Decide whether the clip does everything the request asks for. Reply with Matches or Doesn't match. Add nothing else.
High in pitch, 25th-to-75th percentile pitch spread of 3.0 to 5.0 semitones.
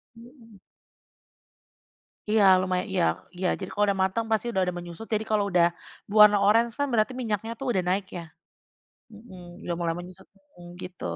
Matches